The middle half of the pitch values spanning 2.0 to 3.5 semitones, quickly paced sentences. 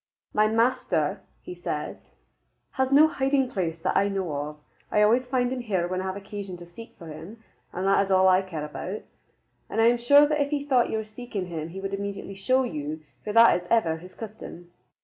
No: average, 5.3 semitones; fast, 220 wpm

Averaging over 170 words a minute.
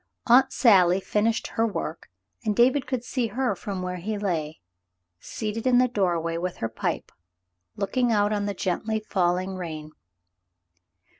No: average, 150 wpm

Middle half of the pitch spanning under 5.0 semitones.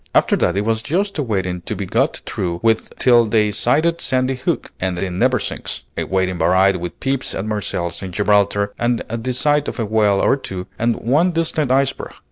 No: average, 5.3 semitones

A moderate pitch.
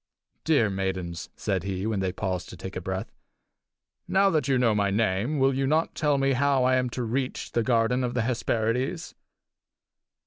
No: low, 120 Hz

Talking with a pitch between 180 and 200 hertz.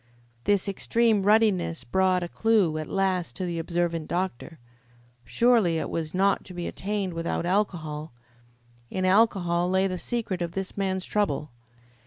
Yes: medium, 185 Hz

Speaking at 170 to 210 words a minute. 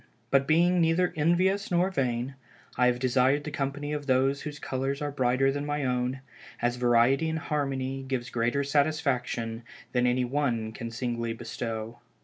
No: average, 160 wpm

